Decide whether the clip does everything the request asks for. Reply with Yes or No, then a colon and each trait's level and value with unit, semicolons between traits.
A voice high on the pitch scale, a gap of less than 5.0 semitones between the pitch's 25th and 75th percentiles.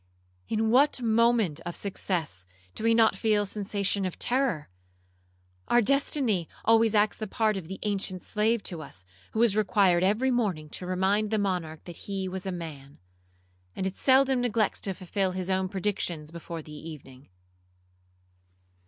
Yes: high, 195 Hz; average, 4.1 semitones